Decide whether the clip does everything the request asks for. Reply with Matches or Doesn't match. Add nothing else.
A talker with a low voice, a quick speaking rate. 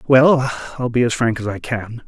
Matches